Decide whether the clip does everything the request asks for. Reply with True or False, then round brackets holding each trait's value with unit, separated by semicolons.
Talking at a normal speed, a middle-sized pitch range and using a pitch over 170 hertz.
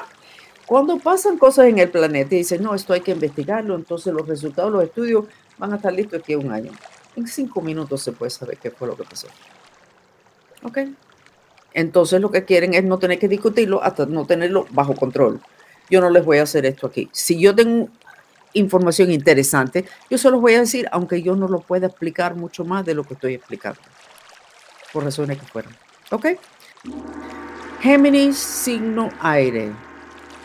False (180 wpm; 6.7 semitones; 185 Hz)